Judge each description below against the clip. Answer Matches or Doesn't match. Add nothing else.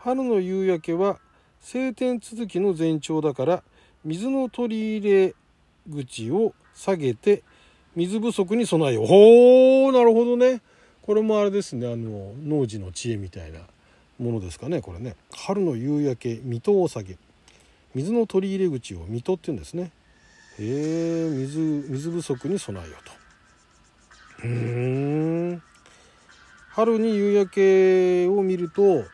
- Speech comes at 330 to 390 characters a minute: Doesn't match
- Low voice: Doesn't match